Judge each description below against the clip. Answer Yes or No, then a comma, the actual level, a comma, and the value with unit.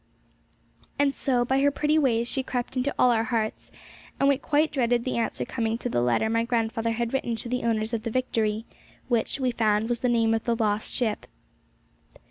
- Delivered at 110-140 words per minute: No, fast, 205 wpm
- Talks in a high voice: Yes, high, 235 Hz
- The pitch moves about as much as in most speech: No, narrow, 2.3 semitones